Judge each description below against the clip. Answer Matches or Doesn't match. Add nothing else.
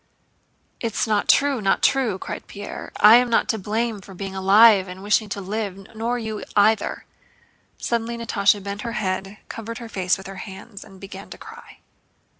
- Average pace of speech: Matches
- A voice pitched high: Matches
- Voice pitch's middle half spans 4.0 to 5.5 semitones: Doesn't match